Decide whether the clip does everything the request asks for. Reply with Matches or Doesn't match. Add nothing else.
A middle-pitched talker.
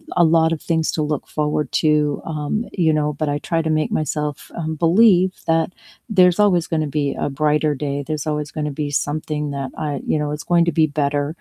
Matches